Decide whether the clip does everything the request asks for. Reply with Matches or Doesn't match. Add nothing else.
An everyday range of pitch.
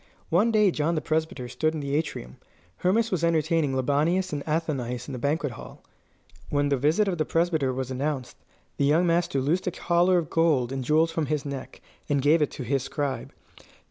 Matches